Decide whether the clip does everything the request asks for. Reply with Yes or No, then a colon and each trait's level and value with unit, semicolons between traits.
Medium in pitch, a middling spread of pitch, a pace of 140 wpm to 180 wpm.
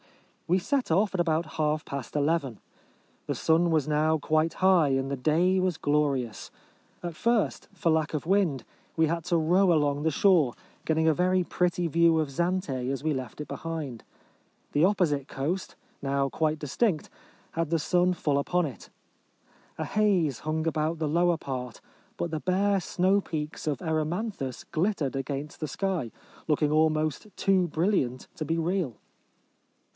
Yes: medium, 160 Hz; average, 3.4 semitones; average, 160 wpm